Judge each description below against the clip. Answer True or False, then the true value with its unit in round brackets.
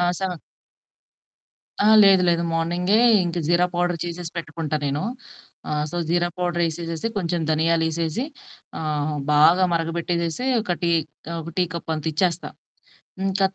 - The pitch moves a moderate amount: False (1.6 semitones)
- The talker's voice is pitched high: False (170 Hz)